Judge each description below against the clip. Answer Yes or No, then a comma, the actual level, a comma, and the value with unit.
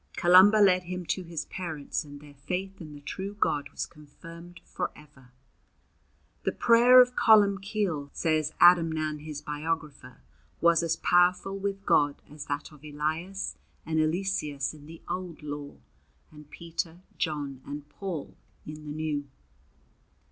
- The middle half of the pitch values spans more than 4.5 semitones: No, average, 3.6 semitones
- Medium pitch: Yes, medium, 160 Hz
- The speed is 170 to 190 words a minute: No, average, 140 wpm